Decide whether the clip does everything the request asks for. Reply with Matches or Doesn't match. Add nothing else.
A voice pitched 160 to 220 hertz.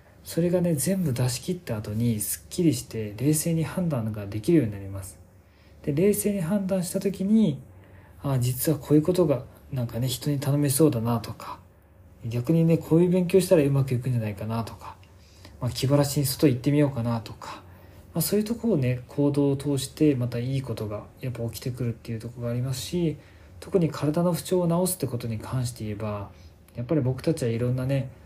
Doesn't match